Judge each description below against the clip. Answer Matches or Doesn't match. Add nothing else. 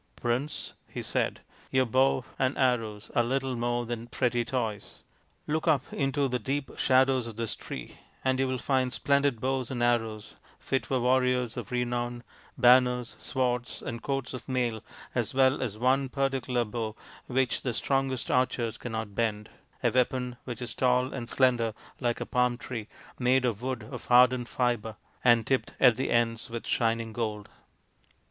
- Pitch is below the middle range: Matches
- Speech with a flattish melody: Matches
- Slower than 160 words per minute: Doesn't match